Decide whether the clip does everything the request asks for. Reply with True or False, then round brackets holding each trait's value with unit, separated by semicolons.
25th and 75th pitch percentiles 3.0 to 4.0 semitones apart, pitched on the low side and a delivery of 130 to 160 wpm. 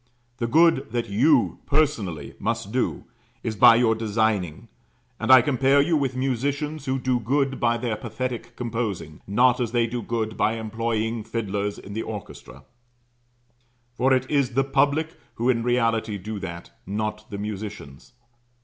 True (3.4 semitones; 115 Hz; 155 wpm)